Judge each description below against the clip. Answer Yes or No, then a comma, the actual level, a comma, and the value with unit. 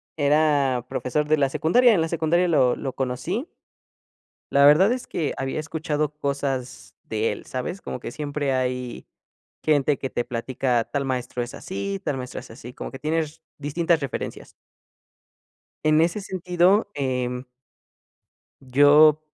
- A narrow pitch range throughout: No, average, 3.9 semitones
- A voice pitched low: No, medium, 145 Hz